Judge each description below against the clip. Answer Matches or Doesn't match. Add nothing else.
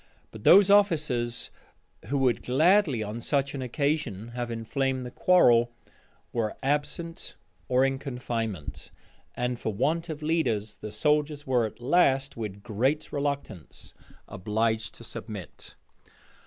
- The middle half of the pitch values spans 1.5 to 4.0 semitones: Doesn't match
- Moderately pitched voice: Doesn't match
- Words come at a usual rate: Doesn't match